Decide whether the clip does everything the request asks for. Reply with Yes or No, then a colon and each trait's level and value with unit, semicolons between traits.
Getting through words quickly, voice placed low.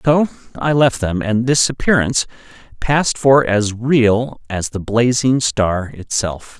No: average, 145 wpm; low, 120 Hz